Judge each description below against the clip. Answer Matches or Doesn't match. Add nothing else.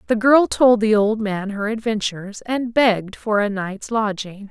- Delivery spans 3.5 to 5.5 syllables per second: Matches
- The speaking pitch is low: Doesn't match